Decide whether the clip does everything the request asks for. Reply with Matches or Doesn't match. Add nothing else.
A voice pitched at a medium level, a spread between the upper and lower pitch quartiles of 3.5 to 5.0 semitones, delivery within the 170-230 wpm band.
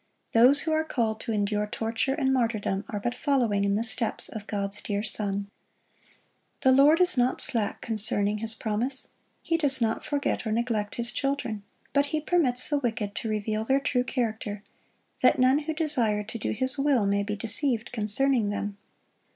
Doesn't match